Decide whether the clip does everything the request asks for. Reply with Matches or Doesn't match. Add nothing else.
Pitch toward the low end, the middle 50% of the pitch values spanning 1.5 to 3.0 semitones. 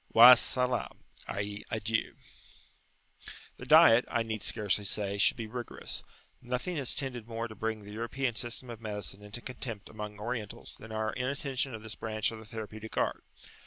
Matches